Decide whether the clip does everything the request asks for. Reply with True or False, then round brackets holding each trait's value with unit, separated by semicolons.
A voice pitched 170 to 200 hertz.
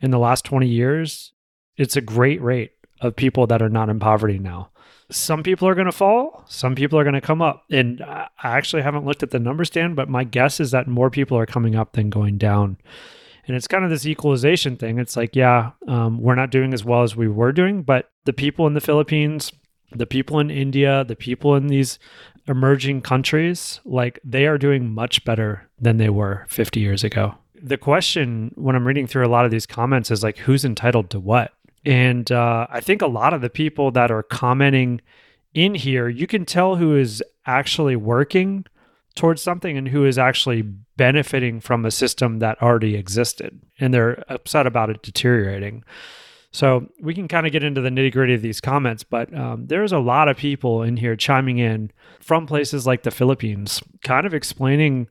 False (130 Hz)